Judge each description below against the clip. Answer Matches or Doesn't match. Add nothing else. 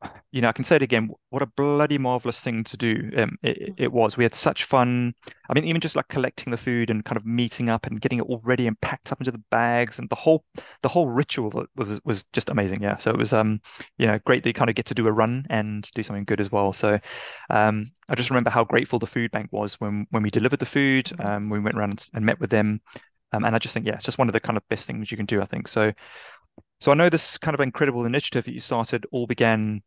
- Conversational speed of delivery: Doesn't match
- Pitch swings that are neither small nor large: Matches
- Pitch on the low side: Matches